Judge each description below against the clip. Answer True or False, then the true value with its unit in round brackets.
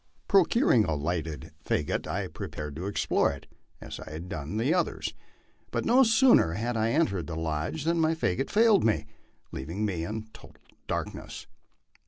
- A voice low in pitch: True (105 Hz)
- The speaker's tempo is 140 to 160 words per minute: False (170 wpm)